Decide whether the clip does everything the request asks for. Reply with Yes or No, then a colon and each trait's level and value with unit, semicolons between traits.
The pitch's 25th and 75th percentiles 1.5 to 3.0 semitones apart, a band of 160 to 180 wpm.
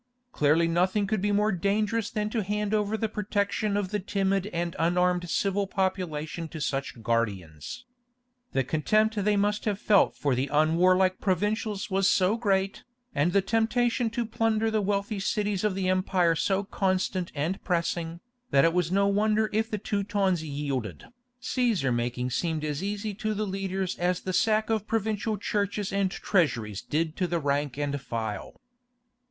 No: average, 4.1 semitones; average, 165 wpm